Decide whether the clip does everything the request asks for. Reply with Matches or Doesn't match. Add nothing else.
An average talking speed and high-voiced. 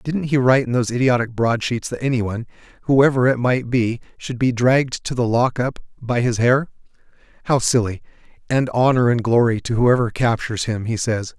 Doesn't match